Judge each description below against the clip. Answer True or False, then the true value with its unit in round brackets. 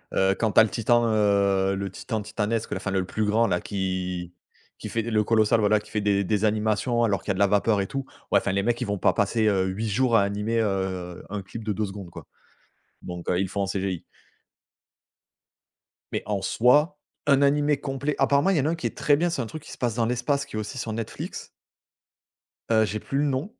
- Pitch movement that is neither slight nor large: True (3.5 semitones)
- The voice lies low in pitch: True (110 Hz)